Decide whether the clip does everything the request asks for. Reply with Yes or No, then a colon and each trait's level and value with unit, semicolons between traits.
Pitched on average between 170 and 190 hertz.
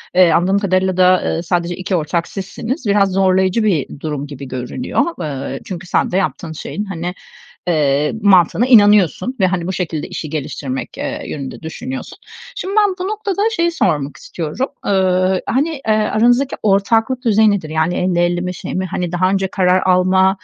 Yes: medium, 185 Hz